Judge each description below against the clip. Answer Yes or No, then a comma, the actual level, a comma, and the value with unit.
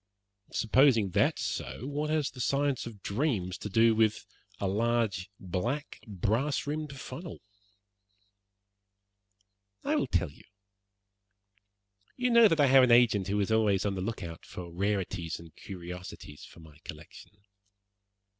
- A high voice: No, low, 110 Hz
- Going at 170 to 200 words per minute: No, average, 145 wpm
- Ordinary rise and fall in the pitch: No, wide, 6.4 semitones